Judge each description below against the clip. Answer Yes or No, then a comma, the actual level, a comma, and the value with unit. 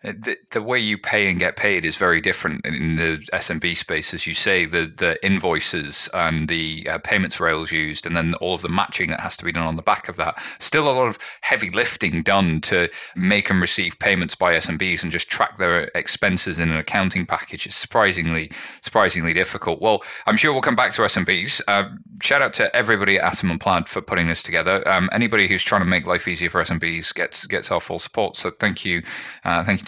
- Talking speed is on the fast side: Yes, fast, 225 wpm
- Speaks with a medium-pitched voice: No, very low, 85 Hz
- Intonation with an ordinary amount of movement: No, narrow, 2.3 semitones